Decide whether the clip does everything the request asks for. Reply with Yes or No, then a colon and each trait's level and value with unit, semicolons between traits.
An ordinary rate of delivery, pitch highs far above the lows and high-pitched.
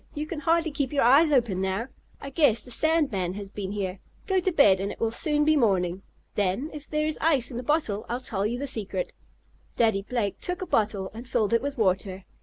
No: fast, 230 wpm; wide, 6.9 semitones; high, 240 Hz